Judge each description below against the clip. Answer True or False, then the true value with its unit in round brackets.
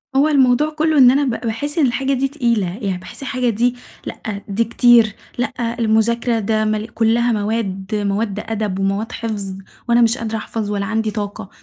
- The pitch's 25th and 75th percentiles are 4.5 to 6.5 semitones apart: False (2.9 semitones)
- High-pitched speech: True (225 Hz)